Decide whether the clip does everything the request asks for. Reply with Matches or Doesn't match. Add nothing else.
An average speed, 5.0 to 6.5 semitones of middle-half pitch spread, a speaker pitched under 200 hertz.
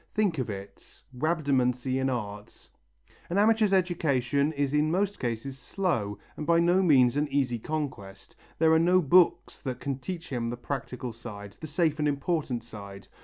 Matches